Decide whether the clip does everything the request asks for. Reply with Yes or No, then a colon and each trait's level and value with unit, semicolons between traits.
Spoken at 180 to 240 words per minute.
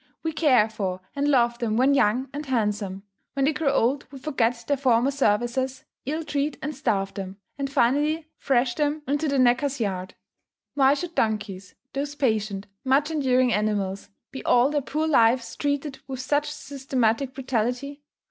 No: average, 165 wpm